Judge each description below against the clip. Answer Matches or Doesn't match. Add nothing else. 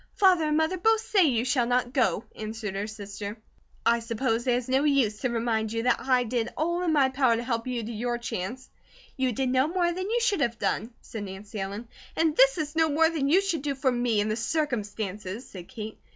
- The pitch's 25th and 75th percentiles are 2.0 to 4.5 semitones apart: Doesn't match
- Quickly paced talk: Matches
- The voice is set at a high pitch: Matches